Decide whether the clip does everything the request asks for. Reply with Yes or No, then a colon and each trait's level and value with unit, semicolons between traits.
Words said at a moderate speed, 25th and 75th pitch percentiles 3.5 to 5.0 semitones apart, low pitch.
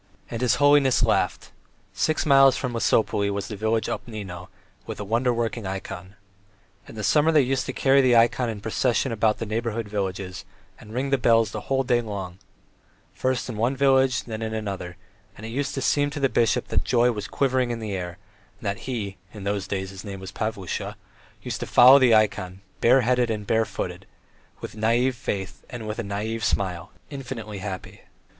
Yes: average, 190 wpm; average, 3.8 semitones; low, 115 Hz